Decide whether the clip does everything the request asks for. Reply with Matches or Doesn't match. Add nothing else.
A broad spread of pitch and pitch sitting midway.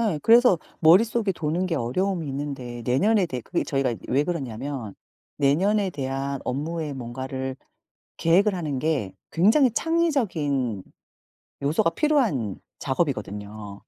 Matches